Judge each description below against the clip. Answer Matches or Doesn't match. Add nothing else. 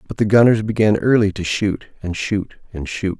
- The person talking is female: Doesn't match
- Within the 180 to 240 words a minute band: Matches